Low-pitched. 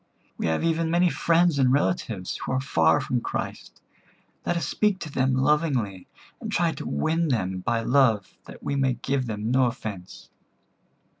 Yes: low, 130 Hz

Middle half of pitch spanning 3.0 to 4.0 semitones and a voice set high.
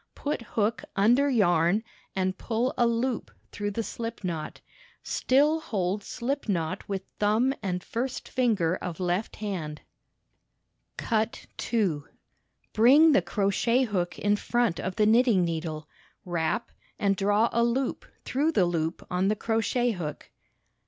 No: average, 4.7 semitones; high, 210 Hz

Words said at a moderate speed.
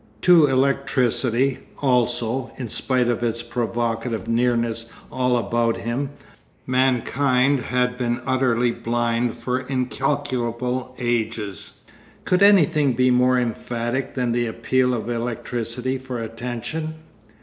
No: slow, 110 wpm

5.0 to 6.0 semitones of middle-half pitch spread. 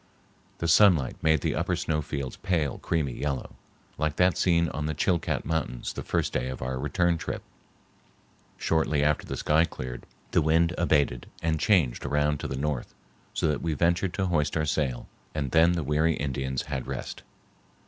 No: average, 3.1 semitones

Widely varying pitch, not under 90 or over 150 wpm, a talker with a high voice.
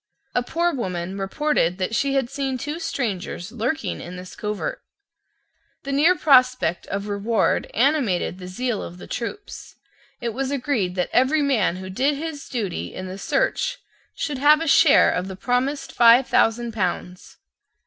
No: wide, 6.7 semitones; average, 160 wpm; high, 240 Hz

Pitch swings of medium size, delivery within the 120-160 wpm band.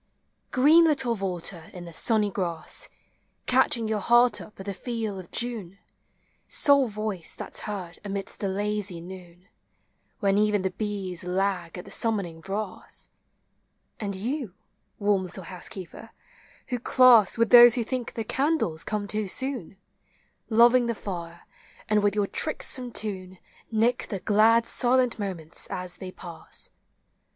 Yes: average, 4.0 semitones; average, 145 wpm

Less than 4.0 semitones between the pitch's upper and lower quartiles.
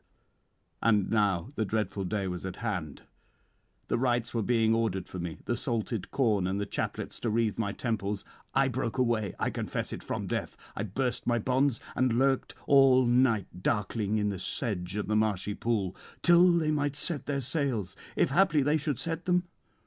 No: average, 4.6 semitones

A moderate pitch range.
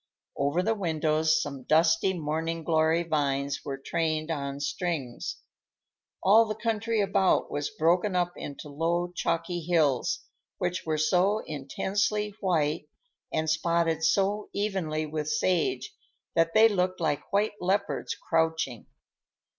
Yes: average, 3.5 semitones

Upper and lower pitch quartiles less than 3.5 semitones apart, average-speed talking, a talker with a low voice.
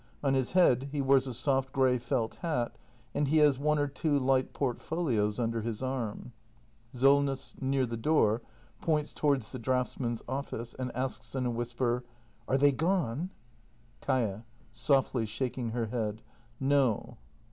Yes: average, 3.0 semitones; average, 150 wpm; low, 130 Hz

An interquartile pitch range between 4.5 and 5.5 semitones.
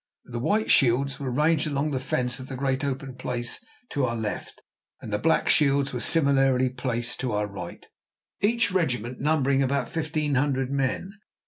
No: average, 2.7 semitones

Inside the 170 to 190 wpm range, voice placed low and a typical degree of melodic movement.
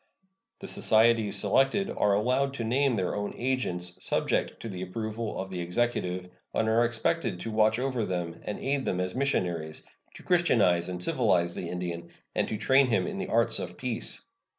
No: average, 180 wpm; low, 110 Hz; wide, 5.9 semitones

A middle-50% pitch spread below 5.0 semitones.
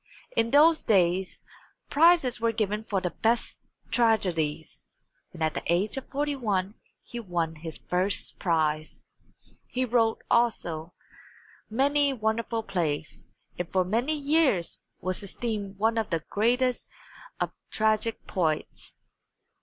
No: average, 5.3 semitones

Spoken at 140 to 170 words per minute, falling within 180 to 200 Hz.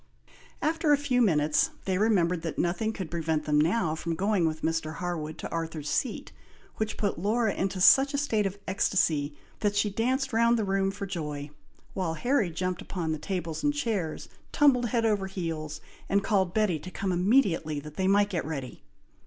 No: average, 185 wpm; high, 190 Hz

